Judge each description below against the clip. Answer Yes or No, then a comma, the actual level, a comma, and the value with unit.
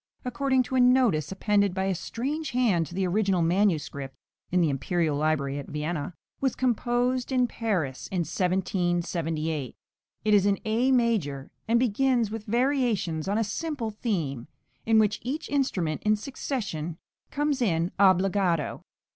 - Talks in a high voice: Yes, high, 200 Hz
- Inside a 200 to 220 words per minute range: No, average, 145 wpm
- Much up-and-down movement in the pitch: Yes, wide, 6.6 semitones